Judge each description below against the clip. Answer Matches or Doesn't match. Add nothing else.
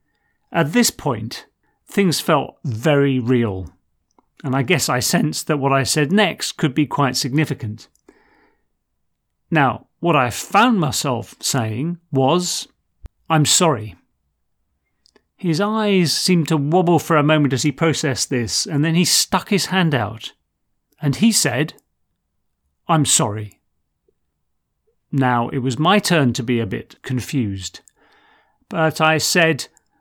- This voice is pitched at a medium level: Matches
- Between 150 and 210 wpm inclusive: Doesn't match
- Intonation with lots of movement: Matches